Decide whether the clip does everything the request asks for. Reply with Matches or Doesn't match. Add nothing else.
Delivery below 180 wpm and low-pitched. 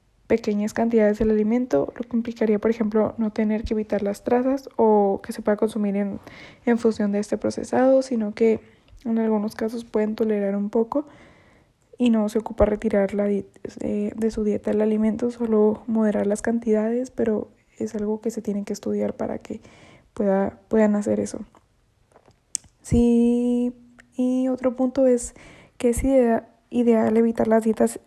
Doesn't match